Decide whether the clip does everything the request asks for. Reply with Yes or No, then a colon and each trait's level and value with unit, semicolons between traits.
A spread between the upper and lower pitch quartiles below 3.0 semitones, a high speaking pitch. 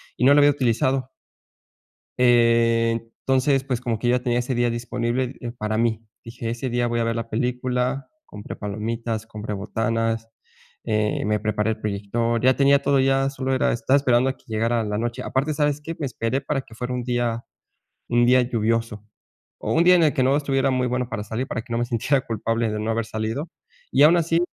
No: narrow, 2.5 semitones; low, 120 Hz